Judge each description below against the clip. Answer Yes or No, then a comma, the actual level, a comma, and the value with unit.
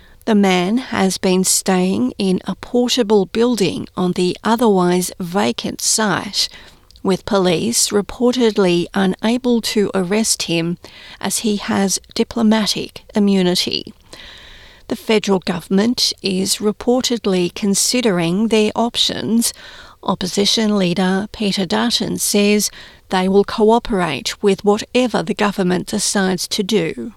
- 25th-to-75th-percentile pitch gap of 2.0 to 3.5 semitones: Yes, average, 2.8 semitones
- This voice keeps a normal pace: No, slow, 110 wpm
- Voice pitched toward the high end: Yes, high, 205 Hz